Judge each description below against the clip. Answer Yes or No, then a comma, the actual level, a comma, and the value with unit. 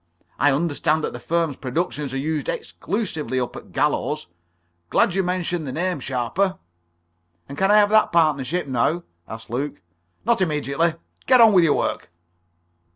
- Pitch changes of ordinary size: Yes, average, 4.6 semitones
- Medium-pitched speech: Yes, medium, 155 Hz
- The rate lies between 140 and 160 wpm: Yes, average, 155 wpm